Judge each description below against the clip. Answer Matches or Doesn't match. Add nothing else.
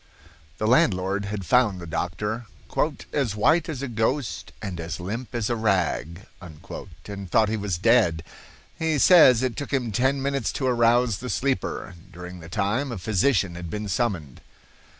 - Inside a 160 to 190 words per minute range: Matches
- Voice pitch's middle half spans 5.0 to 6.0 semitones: Matches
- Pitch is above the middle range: Doesn't match